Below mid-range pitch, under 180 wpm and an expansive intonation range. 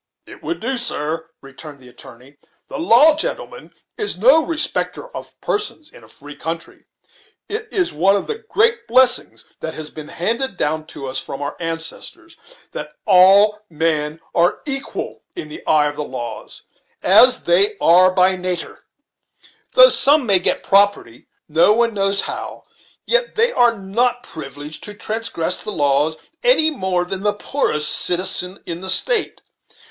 No: high, 190 Hz; average, 160 wpm; wide, 9.0 semitones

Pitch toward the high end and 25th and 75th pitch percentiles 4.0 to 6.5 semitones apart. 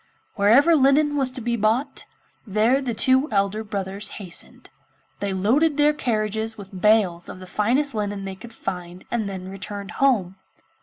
Yes: high, 215 Hz; average, 4.8 semitones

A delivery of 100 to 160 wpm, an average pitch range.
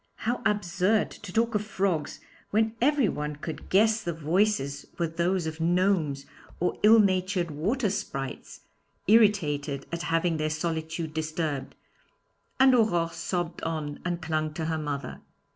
Yes: average, 140 wpm; average, 4.6 semitones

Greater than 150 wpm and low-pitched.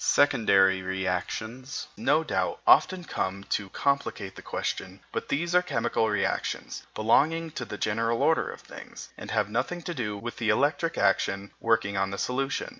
Yes: average, 165 wpm; low, 115 Hz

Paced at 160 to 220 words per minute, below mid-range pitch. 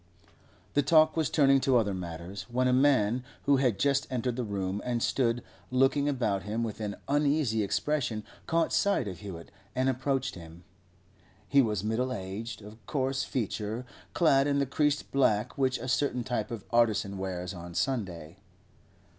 Yes: average, 165 wpm; low, 120 Hz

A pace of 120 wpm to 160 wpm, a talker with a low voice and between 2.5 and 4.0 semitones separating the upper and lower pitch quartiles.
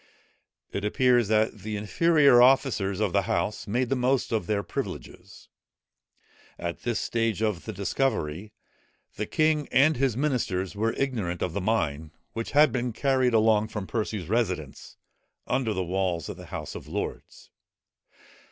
No: average, 150 wpm; low, 110 Hz; average, 4.6 semitones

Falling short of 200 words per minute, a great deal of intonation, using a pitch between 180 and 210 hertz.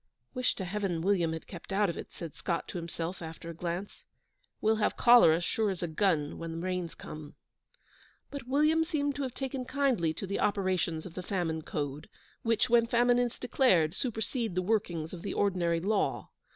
Yes: average, 190 wpm; wide, 5.8 semitones; high, 190 Hz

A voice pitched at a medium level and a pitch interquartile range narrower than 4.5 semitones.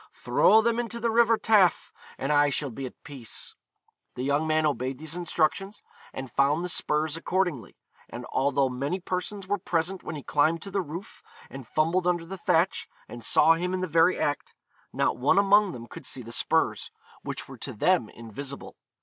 No: medium, 160 Hz; average, 5.2 semitones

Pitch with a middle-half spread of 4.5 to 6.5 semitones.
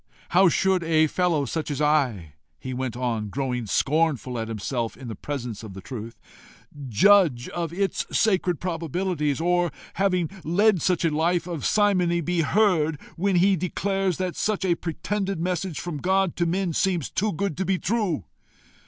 Yes: average, 5.1 semitones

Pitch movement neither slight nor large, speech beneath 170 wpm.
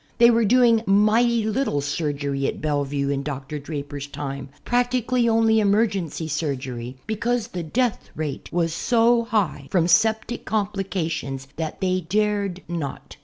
No: wide, 7.6 semitones; slow, 135 wpm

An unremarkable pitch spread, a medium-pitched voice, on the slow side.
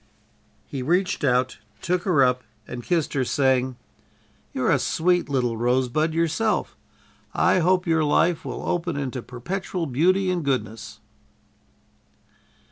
No: wide, 5.7 semitones; medium, 150 Hz; slow, 125 wpm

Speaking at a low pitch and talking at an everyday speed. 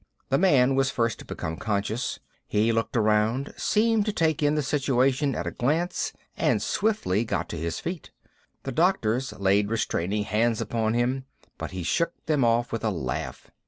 Yes: low, 120 Hz; average, 175 wpm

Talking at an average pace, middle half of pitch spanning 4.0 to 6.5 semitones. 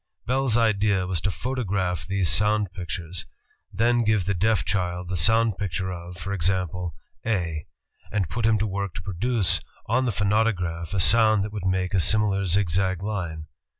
No: average, 170 wpm; average, 3.3 semitones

